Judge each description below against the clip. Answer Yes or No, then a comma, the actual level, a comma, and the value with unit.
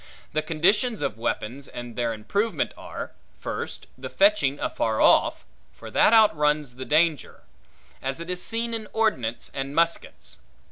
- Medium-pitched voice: Yes, medium, 155 Hz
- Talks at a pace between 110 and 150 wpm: Yes, average, 145 wpm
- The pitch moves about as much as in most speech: No, wide, 8.5 semitones